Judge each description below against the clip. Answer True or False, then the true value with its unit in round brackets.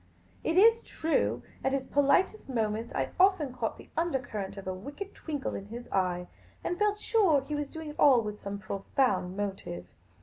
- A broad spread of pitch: True (7.8 semitones)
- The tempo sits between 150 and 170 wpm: False (180 wpm)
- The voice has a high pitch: True (265 Hz)